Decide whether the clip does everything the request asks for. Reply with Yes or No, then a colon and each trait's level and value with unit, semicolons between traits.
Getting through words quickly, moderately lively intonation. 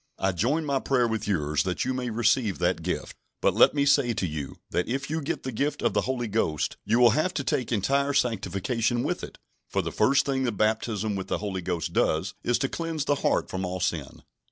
No: fast, 230 wpm; wide, 6.2 semitones